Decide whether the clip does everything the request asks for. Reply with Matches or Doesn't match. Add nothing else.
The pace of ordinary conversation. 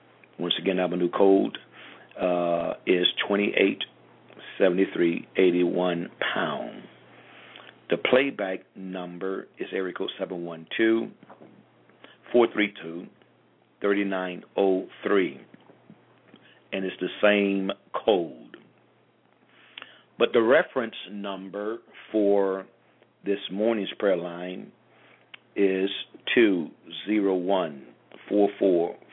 Doesn't match